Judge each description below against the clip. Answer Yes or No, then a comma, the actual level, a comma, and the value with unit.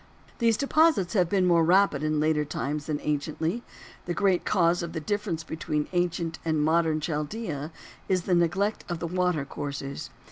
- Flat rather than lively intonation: No, average, 3.1 semitones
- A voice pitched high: No, medium, 170 Hz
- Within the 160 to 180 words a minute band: Yes, average, 170 wpm